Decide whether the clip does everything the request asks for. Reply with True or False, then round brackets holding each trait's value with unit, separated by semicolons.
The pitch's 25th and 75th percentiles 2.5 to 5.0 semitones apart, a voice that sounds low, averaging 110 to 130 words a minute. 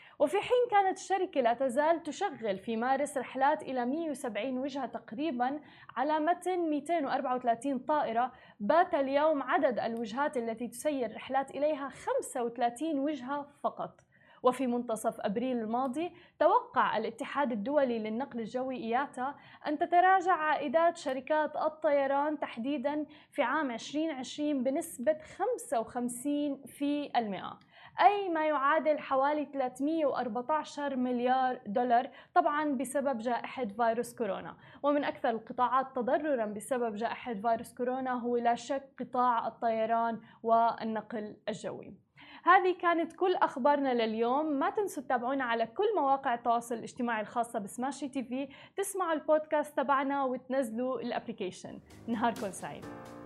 False (4.0 semitones; 270 Hz; 115 wpm)